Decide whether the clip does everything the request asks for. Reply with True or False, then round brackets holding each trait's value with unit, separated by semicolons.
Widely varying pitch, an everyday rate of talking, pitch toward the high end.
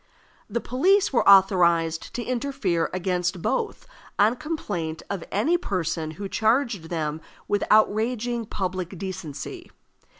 False (5.9 semitones; 120 wpm; 195 Hz)